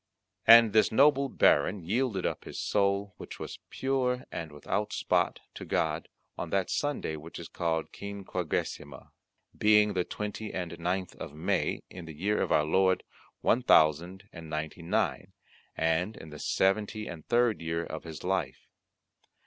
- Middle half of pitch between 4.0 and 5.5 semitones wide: Yes, average, 4.7 semitones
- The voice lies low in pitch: Yes, very low, 95 Hz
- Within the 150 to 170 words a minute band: Yes, average, 160 wpm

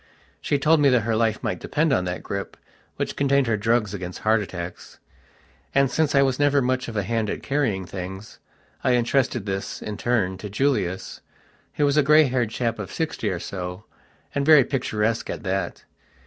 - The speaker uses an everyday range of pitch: No, wide, 5.7 semitones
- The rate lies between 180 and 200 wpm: Yes, average, 190 wpm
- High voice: No, low, 115 Hz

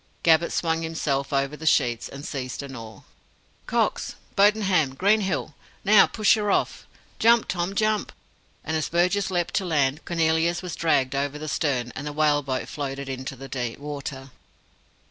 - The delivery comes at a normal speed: Yes, average, 160 wpm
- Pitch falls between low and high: Yes, medium, 155 Hz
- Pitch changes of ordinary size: Yes, average, 4.4 semitones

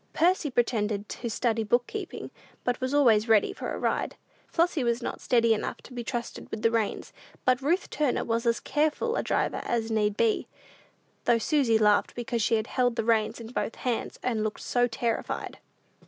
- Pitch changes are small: Yes, narrow, 2.2 semitones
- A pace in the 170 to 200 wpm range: Yes, average, 185 wpm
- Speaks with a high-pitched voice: Yes, high, 235 Hz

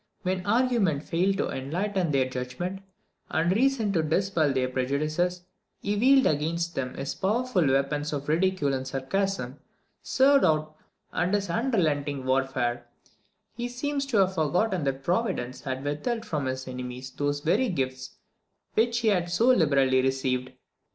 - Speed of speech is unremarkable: Yes, average, 145 wpm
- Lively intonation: Yes, wide, 6.9 semitones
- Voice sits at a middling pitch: Yes, medium, 160 Hz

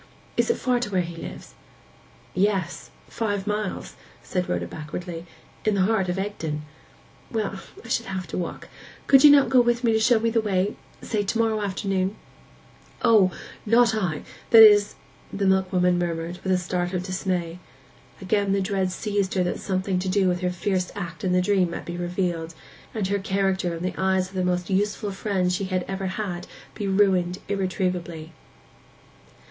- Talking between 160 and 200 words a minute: Yes, average, 175 wpm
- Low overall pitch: No, high, 190 Hz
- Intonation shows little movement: Yes, narrow, 2.3 semitones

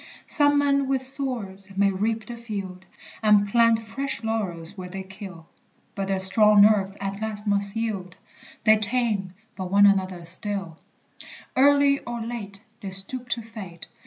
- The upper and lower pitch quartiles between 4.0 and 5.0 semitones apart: No, average, 3.2 semitones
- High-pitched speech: Yes, high, 205 Hz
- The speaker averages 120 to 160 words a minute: Yes, average, 155 wpm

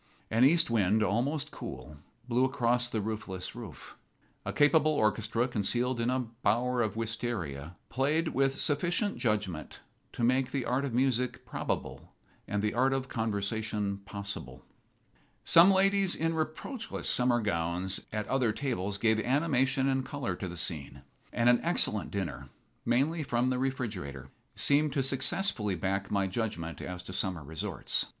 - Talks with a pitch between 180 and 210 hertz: No, low, 120 Hz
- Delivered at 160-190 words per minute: No, average, 150 wpm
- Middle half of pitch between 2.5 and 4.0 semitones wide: No, average, 5.0 semitones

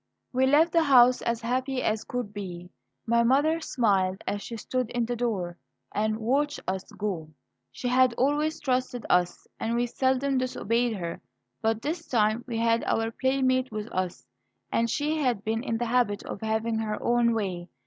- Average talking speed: Yes, average, 180 wpm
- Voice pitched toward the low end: No, high, 235 Hz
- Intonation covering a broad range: No, average, 3.2 semitones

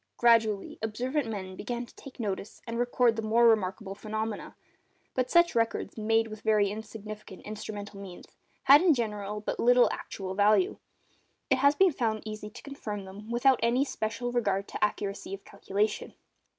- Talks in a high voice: Yes, high, 220 Hz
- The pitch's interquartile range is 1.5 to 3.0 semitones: Yes, narrow, 2.6 semitones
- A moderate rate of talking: Yes, average, 160 wpm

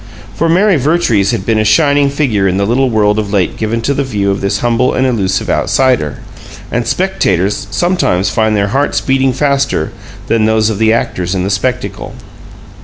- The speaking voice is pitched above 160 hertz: No, low, 115 Hz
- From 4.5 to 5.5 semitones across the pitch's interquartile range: Yes, average, 5.1 semitones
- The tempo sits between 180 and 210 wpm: Yes, average, 185 wpm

